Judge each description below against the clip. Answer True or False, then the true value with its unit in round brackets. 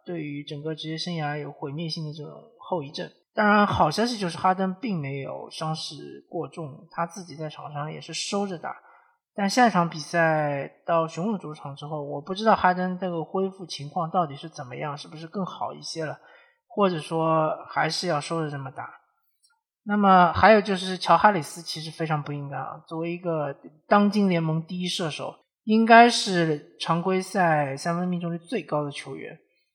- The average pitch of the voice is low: False (170 Hz)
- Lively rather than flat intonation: False (3.6 semitones)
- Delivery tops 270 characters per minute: True (285 characters per minute)